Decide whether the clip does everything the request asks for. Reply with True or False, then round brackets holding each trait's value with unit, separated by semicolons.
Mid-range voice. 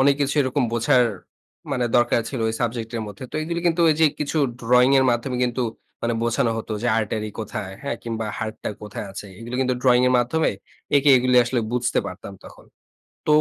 False (120 Hz)